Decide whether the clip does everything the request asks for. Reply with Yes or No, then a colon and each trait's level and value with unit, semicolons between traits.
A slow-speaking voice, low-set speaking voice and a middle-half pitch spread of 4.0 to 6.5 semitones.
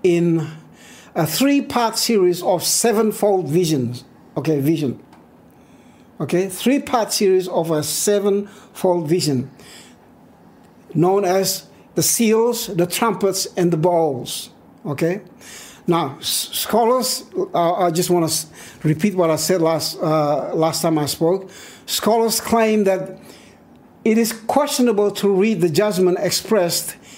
No: slow, 125 wpm; medium, 185 Hz; average, 4.8 semitones